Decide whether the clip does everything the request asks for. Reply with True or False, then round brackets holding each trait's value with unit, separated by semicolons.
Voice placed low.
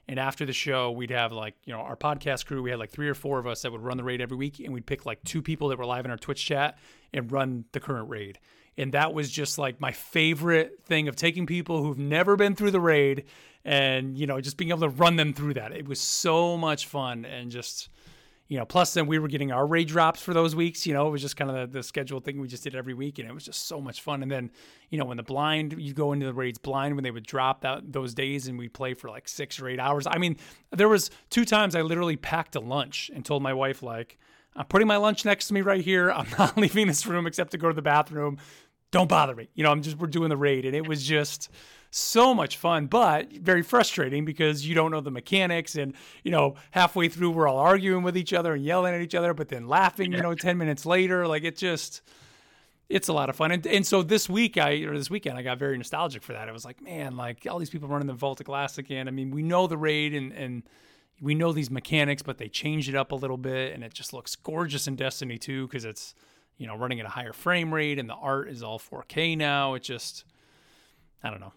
False (145 Hz)